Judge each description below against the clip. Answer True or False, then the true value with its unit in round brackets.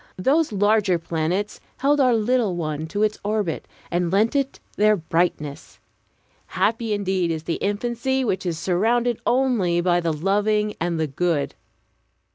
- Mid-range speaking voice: False (200 Hz)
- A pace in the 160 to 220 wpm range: False (145 wpm)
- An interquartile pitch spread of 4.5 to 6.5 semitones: True (4.8 semitones)